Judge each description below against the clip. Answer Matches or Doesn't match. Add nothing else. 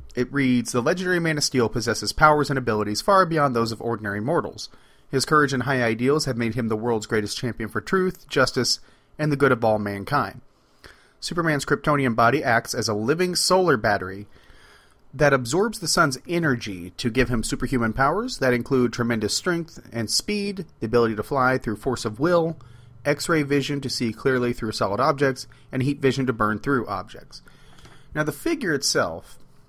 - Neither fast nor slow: Matches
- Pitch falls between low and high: Doesn't match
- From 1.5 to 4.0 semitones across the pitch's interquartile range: Doesn't match